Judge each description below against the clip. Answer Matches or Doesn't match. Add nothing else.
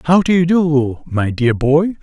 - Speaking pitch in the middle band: Matches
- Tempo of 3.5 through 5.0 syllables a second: Matches